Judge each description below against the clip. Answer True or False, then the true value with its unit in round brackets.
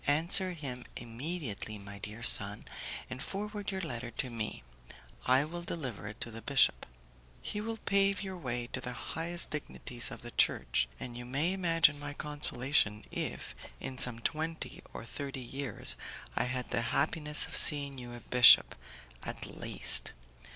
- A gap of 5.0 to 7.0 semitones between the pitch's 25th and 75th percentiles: True (5.4 semitones)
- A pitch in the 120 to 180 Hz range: True (135 Hz)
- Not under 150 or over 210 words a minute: True (160 wpm)